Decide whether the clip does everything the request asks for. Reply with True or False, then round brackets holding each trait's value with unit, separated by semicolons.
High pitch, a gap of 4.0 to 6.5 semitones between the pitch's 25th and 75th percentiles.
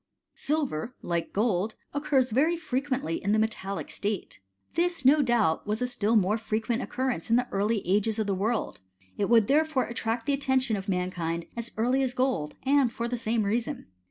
True (230 Hz; 4.3 semitones)